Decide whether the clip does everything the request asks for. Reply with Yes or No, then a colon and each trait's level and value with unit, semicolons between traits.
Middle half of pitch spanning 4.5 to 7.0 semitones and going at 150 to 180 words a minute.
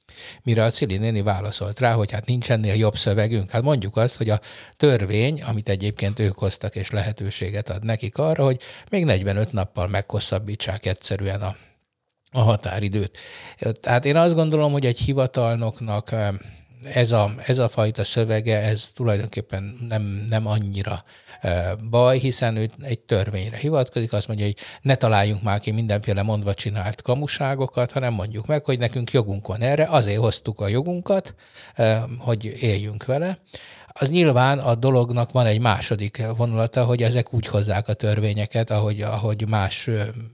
No: average, 3.0 semitones; fast, 155 wpm